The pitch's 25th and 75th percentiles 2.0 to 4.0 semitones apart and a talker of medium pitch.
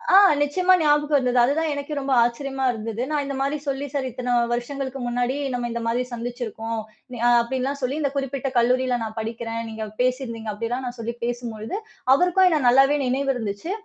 No: average, 3.0 semitones; very high, 250 Hz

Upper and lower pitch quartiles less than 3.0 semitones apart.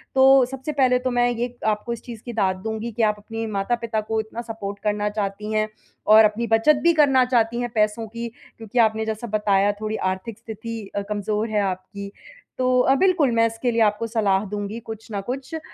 Yes: narrow, 2.4 semitones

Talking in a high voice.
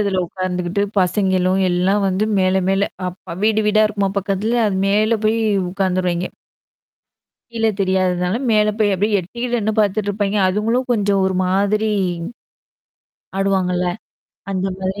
Yes: high, 195 Hz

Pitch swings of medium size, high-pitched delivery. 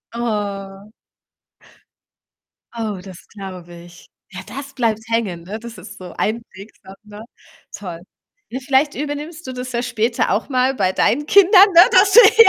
No: wide, 5.8 semitones; high, 230 Hz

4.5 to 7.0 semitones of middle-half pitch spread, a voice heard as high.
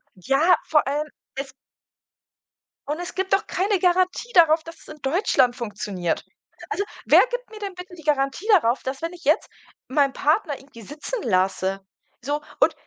Yes: average, 5.3 semitones; very high, 300 Hz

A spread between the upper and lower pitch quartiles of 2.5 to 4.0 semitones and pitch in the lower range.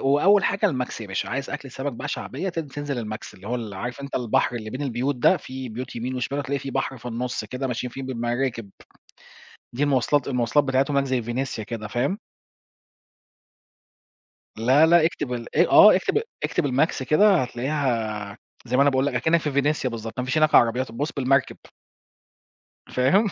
Yes: average, 3.2 semitones; low, 130 Hz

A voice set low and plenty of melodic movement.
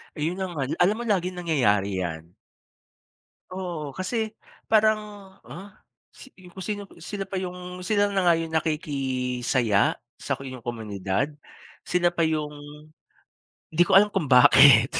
No: medium, 155 Hz; wide, 6.7 semitones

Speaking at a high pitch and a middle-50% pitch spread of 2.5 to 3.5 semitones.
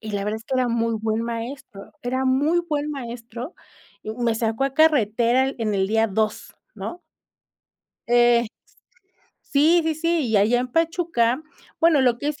No: high, 240 Hz; average, 4.5 semitones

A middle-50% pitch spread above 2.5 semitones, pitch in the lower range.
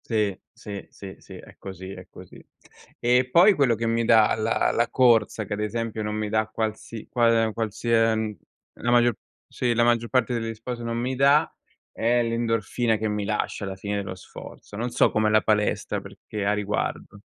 No: narrow, 2.0 semitones; low, 115 Hz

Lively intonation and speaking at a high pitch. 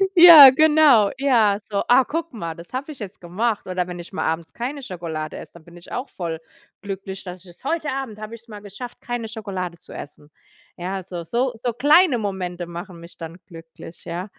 Yes: wide, 6.1 semitones; high, 200 Hz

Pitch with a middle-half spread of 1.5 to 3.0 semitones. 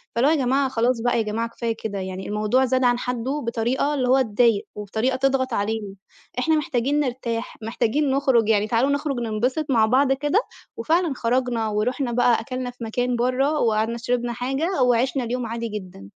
Yes: average, 2.7 semitones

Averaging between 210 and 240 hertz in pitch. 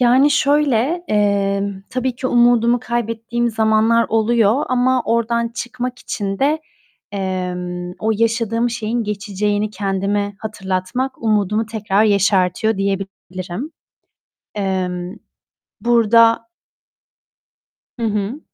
Yes: high, 220 Hz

